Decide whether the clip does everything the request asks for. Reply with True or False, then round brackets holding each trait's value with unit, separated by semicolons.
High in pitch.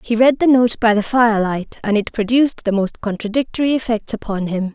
True (225 Hz)